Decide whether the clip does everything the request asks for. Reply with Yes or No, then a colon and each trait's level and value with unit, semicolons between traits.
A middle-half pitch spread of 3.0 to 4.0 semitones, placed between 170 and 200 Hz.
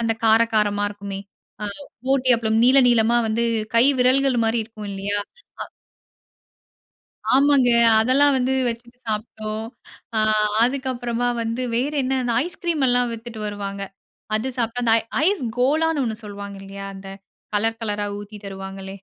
No: average, 3.5 semitones; high, 230 Hz